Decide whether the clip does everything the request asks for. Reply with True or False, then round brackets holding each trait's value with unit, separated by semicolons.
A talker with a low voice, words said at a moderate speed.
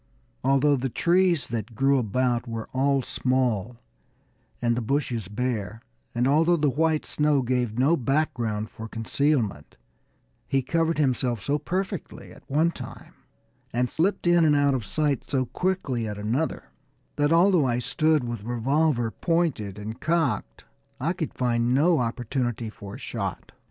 True (130 Hz; 150 wpm)